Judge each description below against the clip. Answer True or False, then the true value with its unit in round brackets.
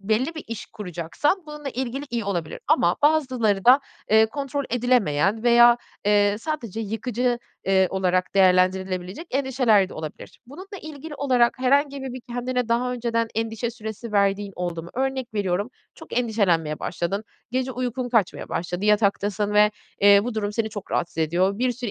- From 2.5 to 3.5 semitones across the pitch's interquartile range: False (4.4 semitones)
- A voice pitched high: True (225 Hz)